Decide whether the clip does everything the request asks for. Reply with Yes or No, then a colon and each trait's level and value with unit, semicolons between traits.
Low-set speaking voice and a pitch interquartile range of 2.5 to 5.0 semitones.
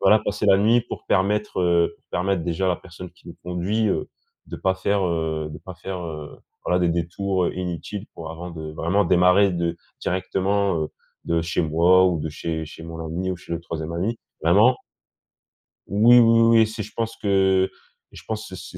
Yes: very low, 90 Hz; average, 3.2 semitones